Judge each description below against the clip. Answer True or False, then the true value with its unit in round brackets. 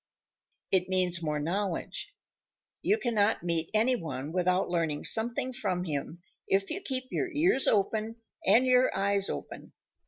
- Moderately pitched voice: False (195 Hz)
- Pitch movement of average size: False (5.7 semitones)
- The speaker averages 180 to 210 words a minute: False (145 wpm)